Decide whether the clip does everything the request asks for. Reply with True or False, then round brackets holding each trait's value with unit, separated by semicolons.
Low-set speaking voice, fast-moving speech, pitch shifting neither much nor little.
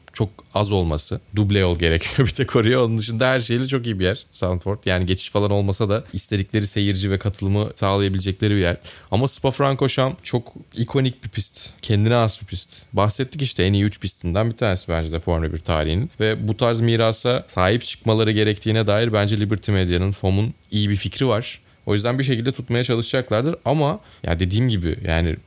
True (105 Hz; 190 wpm; 3.6 semitones)